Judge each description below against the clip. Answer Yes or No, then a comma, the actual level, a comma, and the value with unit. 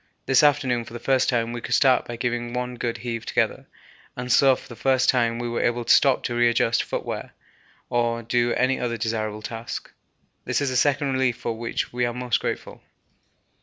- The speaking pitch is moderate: No, low, 120 Hz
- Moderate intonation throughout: No, narrow, 1.5 semitones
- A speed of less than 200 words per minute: No, fast, 205 wpm